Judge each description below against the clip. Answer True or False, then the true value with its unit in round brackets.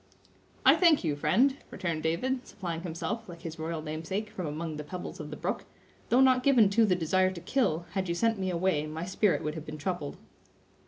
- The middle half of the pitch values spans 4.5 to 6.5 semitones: True (4.9 semitones)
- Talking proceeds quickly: True (210 wpm)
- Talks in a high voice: False (175 Hz)